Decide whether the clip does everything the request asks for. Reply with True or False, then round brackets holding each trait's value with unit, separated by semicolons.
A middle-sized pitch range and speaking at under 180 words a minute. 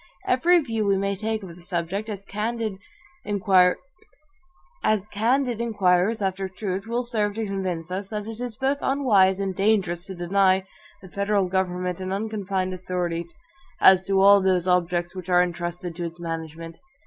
True (3.2 semitones; 155 wpm)